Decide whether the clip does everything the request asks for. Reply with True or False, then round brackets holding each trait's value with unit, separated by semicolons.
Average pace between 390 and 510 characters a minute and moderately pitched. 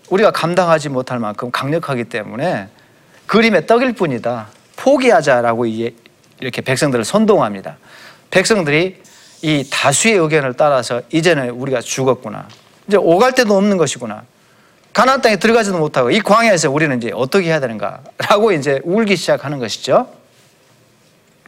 False (345 characters per minute; 160 Hz)